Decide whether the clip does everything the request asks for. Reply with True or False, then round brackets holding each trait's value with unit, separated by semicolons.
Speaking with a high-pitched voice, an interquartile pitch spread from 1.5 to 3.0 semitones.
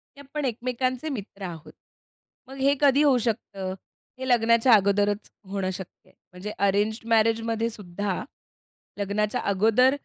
False (220 Hz; 4.0 semitones)